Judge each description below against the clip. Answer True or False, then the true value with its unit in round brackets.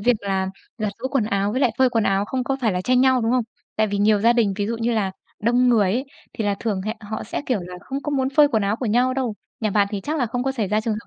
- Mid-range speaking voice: False (225 Hz)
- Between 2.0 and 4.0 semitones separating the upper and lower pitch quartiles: True (3.6 semitones)